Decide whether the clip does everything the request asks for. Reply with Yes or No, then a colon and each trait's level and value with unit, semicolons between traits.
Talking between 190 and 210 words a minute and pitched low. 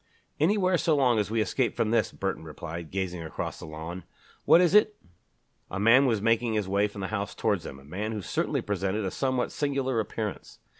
Yes: fast, 205 wpm; low, 110 Hz